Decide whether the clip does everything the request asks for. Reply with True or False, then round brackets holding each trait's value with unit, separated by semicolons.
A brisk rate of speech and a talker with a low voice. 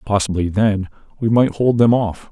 False (180 wpm; 105 Hz)